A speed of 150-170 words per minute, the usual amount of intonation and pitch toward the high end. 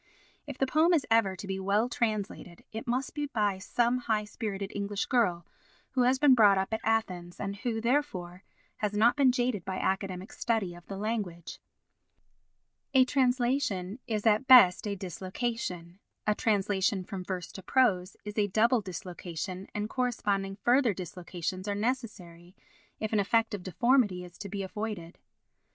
Yes: average, 165 wpm; average, 4.1 semitones; high, 205 Hz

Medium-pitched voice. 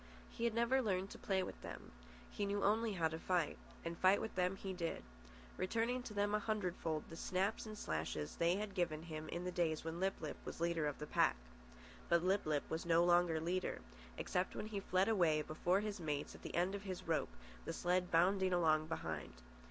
Yes: medium, 180 Hz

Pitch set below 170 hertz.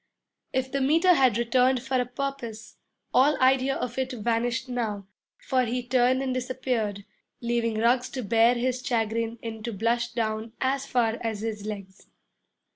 No: high, 240 Hz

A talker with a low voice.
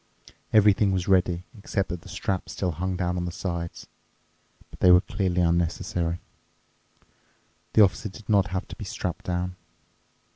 Yes: very low, 90 Hz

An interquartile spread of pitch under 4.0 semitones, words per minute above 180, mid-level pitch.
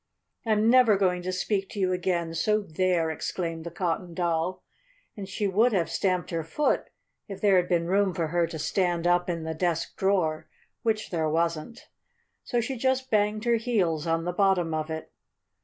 Yes: average, 3.6 semitones; average, 190 wpm; medium, 180 Hz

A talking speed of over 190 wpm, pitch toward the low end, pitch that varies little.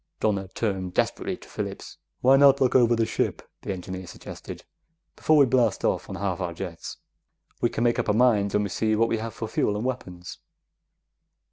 No: average, 200 wpm; low, 110 Hz; average, 4.2 semitones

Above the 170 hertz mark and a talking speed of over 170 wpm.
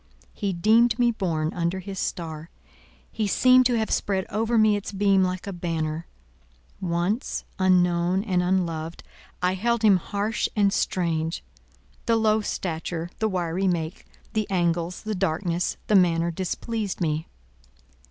No: medium, 185 Hz; average, 140 wpm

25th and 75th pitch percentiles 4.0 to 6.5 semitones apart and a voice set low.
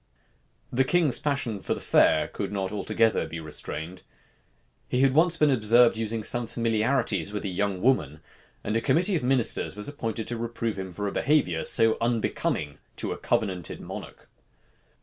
Yes: average, 4.4 semitones; low, 115 Hz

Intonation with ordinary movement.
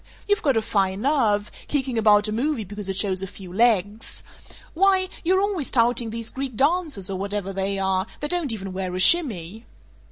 No: wide, 6.4 semitones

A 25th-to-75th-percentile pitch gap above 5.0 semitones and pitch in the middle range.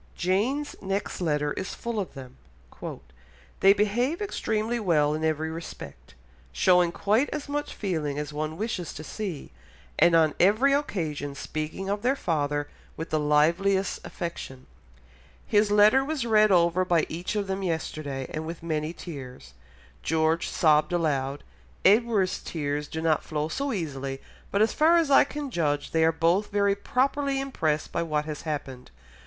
Yes: wide, 5.6 semitones; medium, 170 Hz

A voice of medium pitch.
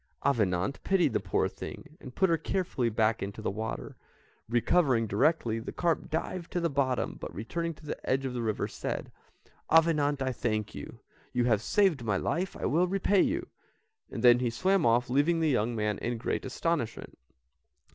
No: low, 130 Hz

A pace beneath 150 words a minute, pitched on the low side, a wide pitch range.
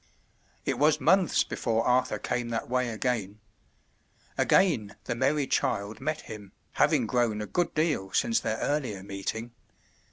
Yes: average, 140 wpm; low, 120 Hz; wide, 5.7 semitones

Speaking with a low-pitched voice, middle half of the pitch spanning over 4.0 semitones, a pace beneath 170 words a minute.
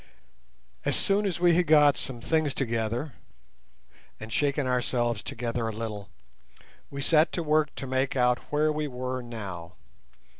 Yes: low, 130 Hz; average, 4.5 semitones; average, 150 wpm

